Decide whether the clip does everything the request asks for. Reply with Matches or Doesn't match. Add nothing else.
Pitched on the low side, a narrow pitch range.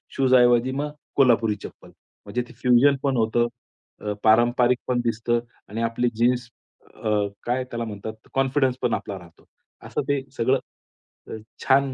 Matches